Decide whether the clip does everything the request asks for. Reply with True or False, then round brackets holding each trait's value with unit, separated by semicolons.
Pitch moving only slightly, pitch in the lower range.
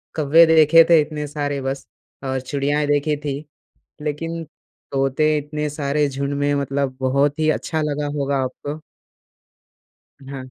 False (1.6 semitones; 145 Hz)